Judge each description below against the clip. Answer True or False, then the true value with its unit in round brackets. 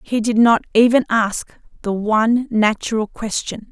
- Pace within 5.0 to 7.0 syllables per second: False (4.4 syllables/s)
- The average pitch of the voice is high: True (220 Hz)